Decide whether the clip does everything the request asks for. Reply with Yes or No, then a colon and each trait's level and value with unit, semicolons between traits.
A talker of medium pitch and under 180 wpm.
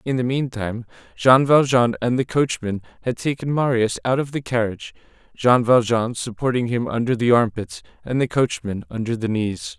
No: low, 120 Hz; average, 170 wpm